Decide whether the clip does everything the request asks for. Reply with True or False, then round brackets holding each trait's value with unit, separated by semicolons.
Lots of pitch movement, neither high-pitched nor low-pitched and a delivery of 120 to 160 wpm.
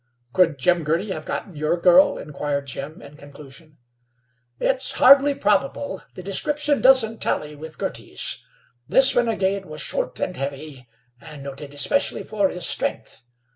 True (6.5 semitones; 170 Hz; 140 wpm)